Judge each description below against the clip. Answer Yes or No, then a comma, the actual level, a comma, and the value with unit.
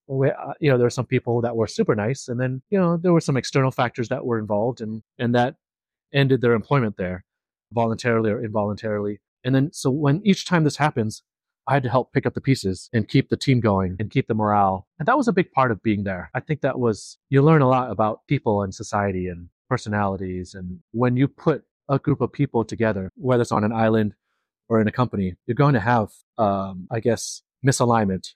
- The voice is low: Yes, low, 120 Hz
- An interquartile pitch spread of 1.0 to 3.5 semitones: No, average, 4.1 semitones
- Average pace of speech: No, fast, 225 wpm